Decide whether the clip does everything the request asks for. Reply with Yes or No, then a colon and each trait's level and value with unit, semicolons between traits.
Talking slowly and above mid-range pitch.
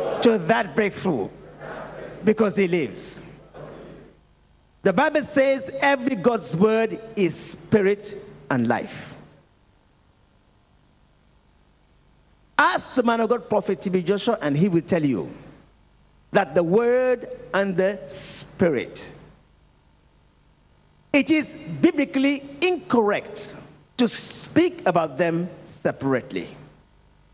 Yes: slow, 95 wpm; high, 195 Hz